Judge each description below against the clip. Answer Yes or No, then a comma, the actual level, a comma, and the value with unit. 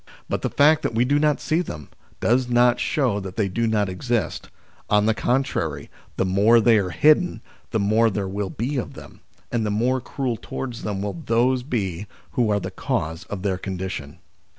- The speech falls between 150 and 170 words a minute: No, average, 195 wpm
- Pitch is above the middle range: No, low, 110 Hz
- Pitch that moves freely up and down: No, average, 4.2 semitones